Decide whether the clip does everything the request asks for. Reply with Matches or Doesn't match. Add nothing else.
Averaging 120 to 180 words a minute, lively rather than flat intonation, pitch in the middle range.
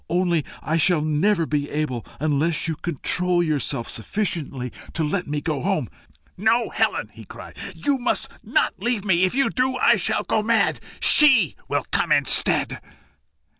Matches